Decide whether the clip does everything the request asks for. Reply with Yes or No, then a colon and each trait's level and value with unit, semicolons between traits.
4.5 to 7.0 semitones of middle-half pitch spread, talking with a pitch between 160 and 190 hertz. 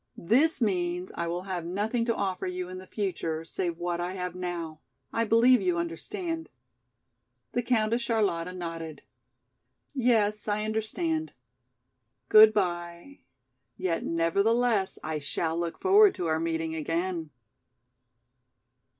Yes: average, 4.8 semitones; medium, 185 Hz